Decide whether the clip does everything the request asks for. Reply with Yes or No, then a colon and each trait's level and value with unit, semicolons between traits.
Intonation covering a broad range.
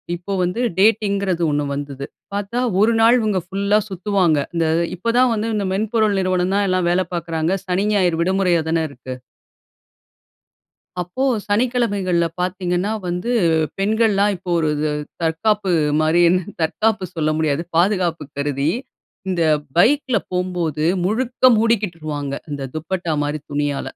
No: average, 4.2 semitones